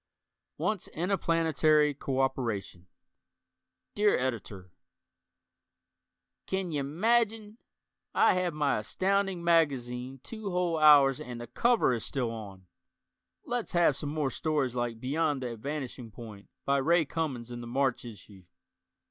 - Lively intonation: Yes, wide, 5.9 semitones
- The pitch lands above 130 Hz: Yes, medium, 140 Hz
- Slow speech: Yes, slow, 125 wpm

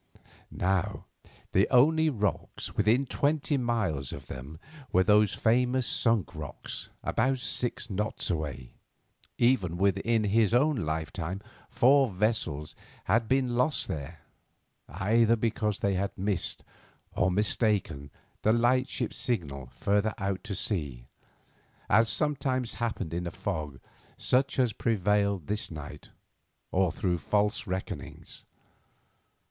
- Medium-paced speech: No, slow, 120 wpm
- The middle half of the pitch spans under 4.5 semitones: No, average, 5.1 semitones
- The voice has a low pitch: Yes, low, 105 Hz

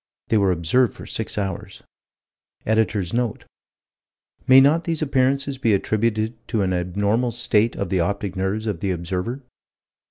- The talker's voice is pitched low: Yes, low, 110 Hz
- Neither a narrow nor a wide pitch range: Yes, average, 4.3 semitones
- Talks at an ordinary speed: Yes, average, 150 wpm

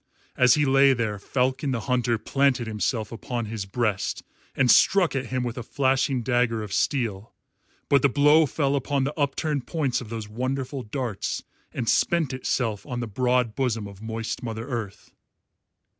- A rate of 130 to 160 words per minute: No, average, 170 wpm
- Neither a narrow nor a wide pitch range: Yes, average, 3.3 semitones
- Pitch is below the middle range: Yes, low, 125 Hz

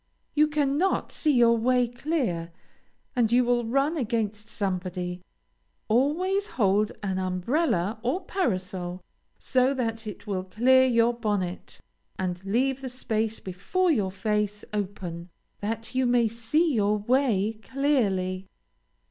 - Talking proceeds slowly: Yes, slow, 125 wpm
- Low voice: No, high, 225 Hz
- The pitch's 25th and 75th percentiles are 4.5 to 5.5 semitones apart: Yes, average, 5.1 semitones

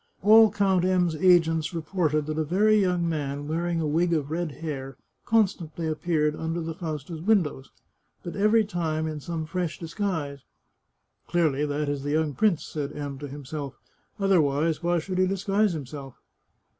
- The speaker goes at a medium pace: Yes, average, 175 wpm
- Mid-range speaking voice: Yes, medium, 160 Hz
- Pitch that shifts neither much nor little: Yes, average, 3.4 semitones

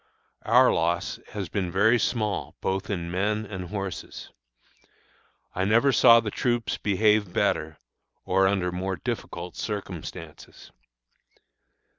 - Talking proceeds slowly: Yes, slow, 115 wpm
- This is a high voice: No, very low, 95 Hz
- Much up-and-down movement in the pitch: No, average, 3.1 semitones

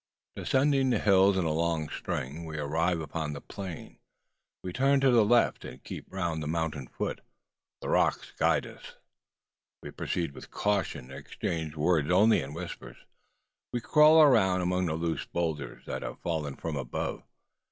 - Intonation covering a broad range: No, average, 4.8 semitones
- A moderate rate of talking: Yes, average, 170 wpm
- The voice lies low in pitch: Yes, very low, 85 Hz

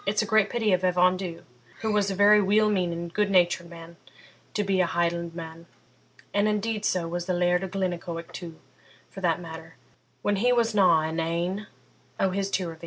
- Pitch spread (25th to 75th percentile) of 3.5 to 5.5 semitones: No, average, 3.1 semitones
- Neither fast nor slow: Yes, average, 185 wpm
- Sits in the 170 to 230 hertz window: Yes, medium, 185 Hz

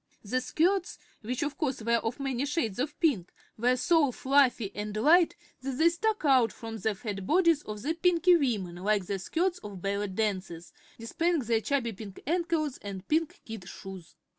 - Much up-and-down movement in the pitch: Yes, wide, 7.2 semitones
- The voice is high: Yes, very high, 250 Hz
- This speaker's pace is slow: No, average, 180 wpm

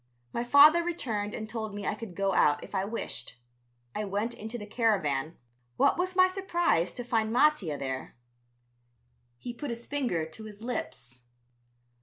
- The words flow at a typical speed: Yes, average, 165 wpm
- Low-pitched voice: No, high, 220 Hz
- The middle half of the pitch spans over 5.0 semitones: Yes, wide, 5.4 semitones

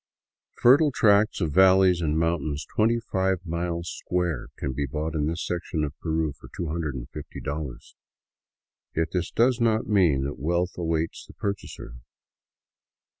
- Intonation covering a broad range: No, average, 3.8 semitones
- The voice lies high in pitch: No, very low, 85 Hz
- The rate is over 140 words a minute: No, slow, 135 wpm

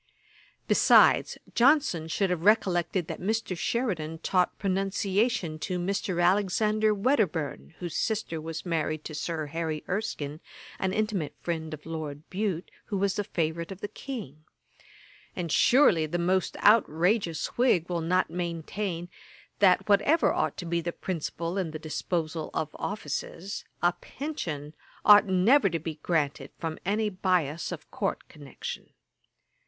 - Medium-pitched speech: Yes, medium, 175 Hz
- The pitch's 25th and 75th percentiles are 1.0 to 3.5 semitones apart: No, average, 4.0 semitones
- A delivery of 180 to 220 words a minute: No, average, 140 wpm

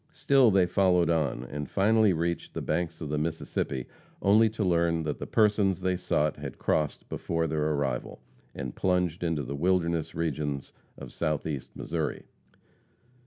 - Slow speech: No, average, 155 wpm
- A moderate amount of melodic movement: Yes, average, 3.6 semitones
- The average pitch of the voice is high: No, very low, 85 Hz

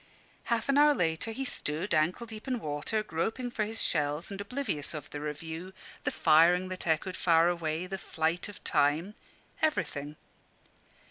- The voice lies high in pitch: No, medium, 175 Hz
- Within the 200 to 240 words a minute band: No, average, 160 wpm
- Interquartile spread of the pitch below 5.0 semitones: No, wide, 5.6 semitones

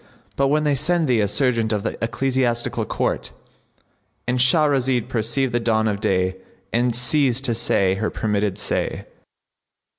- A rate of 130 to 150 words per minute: Yes, average, 145 wpm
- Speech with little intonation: No, average, 3.4 semitones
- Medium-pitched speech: No, low, 120 Hz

